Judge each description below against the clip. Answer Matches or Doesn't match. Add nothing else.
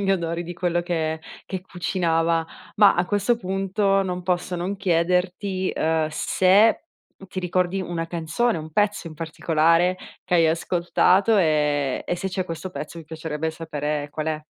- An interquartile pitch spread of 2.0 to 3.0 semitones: Matches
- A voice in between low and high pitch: Matches